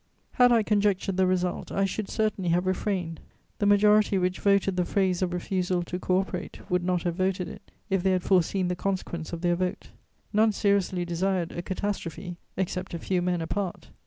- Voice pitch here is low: No, medium, 185 Hz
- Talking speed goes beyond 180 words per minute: Yes, average, 190 wpm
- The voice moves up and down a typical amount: No, narrow, 1.8 semitones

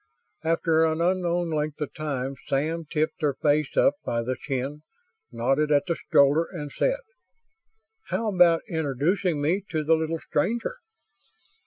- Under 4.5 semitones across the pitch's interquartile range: Yes, average, 3.0 semitones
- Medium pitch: Yes, medium, 155 Hz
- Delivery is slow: No, average, 145 wpm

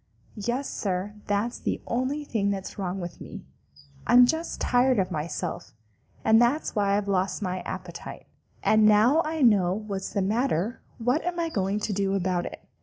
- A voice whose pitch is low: No, high, 210 Hz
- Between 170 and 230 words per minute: Yes, average, 175 wpm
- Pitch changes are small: No, average, 4.3 semitones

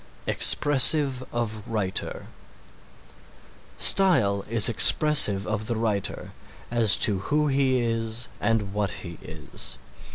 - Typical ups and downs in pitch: Yes, average, 4.0 semitones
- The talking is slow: Yes, slow, 105 wpm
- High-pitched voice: No, low, 115 Hz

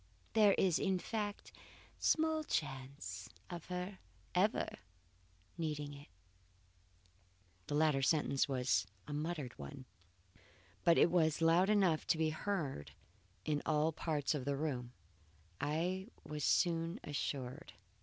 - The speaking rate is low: Yes, slow, 125 wpm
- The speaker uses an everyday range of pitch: Yes, average, 4.2 semitones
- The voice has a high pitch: No, medium, 155 Hz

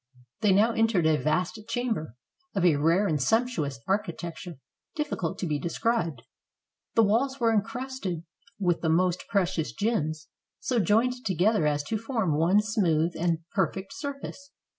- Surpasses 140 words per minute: Yes, average, 150 wpm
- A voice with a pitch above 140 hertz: Yes, high, 190 Hz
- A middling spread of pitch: No, wide, 5.7 semitones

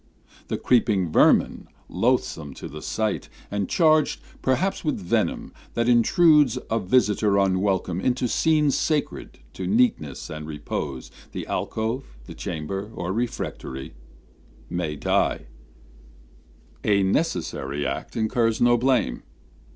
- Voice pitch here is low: Yes, low, 105 Hz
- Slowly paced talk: Yes, slow, 115 wpm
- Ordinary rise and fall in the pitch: No, wide, 6.2 semitones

